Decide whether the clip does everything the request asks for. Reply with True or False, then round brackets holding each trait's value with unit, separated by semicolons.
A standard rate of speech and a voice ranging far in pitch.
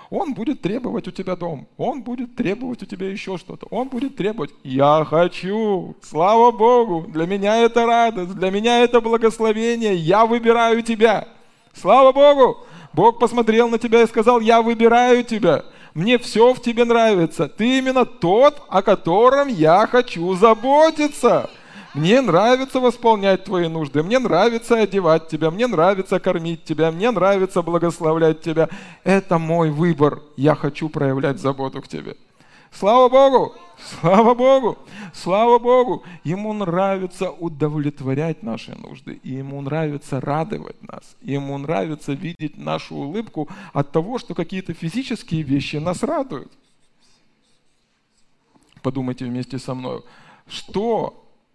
True (135 wpm; 6.7 semitones)